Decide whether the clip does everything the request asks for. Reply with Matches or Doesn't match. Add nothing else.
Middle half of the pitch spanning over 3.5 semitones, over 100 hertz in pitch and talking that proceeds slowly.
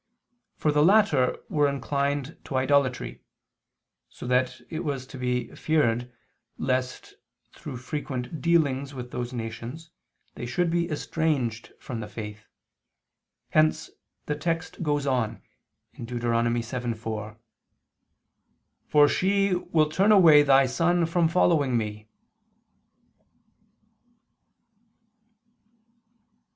Matches